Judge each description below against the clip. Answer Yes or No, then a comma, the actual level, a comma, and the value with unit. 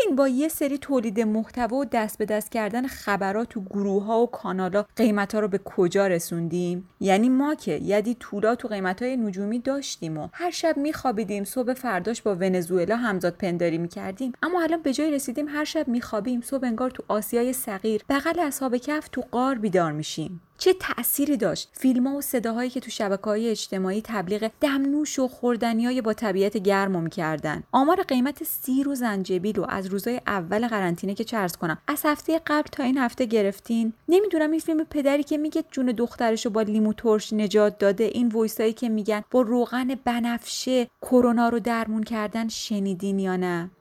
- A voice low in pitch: No, high, 230 Hz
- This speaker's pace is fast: Yes, fast, 180 wpm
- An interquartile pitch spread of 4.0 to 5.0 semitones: Yes, average, 4.6 semitones